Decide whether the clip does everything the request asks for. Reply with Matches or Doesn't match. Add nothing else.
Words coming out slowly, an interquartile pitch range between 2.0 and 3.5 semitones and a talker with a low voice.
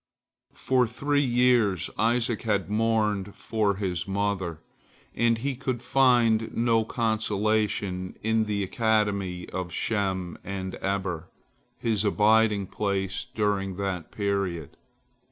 Matches